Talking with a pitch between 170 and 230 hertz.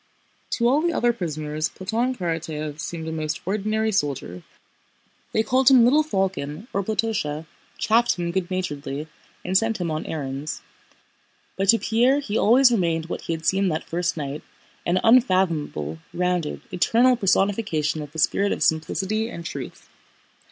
Yes: medium, 185 Hz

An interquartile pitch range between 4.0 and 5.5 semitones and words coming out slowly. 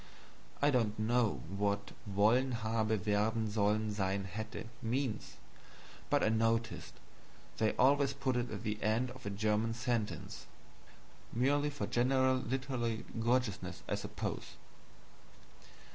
No: average, 3.2 semitones; slow, 120 wpm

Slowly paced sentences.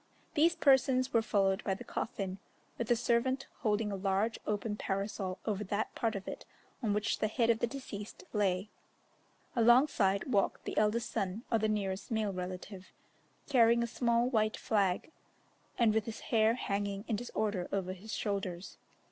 No: average, 165 wpm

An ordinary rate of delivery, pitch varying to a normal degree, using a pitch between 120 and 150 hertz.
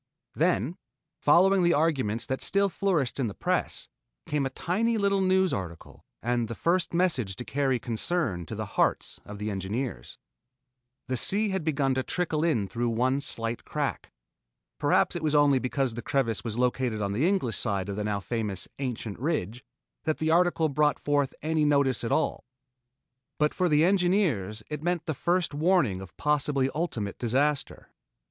No: average, 170 wpm; wide, 6.4 semitones; medium, 140 Hz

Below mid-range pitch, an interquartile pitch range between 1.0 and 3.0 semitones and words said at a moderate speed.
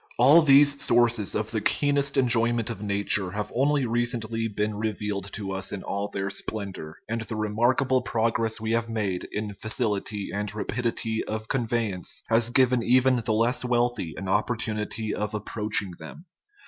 Yes: low, 110 Hz; narrow, 2.6 semitones; average, 160 wpm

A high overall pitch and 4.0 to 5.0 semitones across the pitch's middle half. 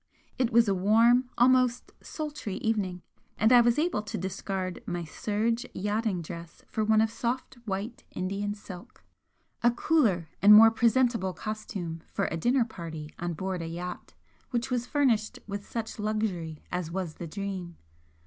Yes: high, 210 Hz; average, 4.5 semitones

